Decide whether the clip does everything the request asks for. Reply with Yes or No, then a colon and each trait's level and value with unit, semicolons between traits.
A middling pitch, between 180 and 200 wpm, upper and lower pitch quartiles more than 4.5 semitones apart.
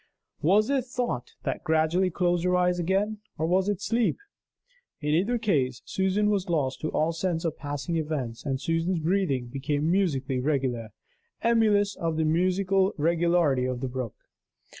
No: medium, 170 Hz; average, 160 wpm; average, 4.9 semitones